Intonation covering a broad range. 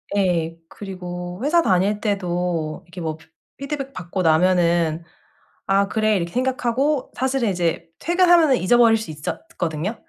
Yes: wide, 6.4 semitones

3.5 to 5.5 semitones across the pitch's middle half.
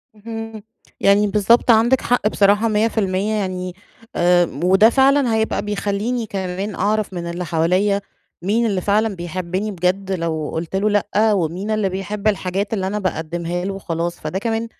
No: average, 3.0 semitones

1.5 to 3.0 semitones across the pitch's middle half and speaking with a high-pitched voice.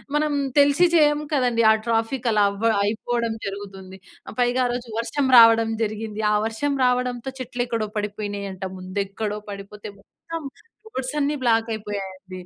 No: average, 3.6 semitones; high, 225 Hz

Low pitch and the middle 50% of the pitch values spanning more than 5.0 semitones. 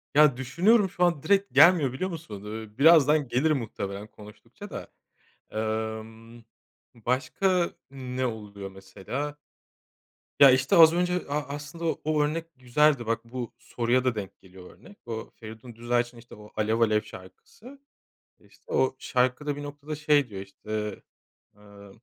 Yes: low, 125 Hz; wide, 5.5 semitones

